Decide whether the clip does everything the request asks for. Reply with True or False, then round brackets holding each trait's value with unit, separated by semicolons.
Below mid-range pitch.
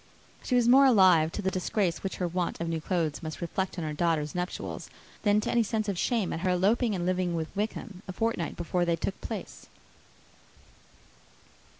False (185 Hz)